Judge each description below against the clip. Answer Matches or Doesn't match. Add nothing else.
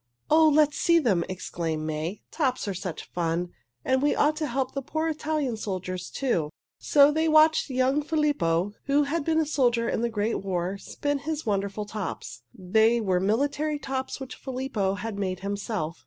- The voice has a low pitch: Doesn't match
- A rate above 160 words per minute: Matches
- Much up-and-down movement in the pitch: Matches